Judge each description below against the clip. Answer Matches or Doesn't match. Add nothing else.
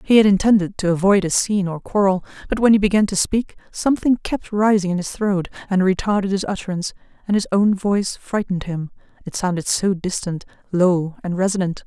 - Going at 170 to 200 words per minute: Matches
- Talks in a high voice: Matches